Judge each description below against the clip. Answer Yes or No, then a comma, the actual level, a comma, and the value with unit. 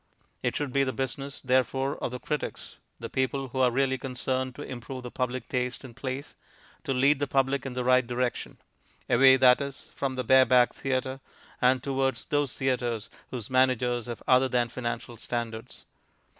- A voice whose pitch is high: No, low, 130 Hz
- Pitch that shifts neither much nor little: No, narrow, 1.3 semitones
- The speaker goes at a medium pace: Yes, average, 175 wpm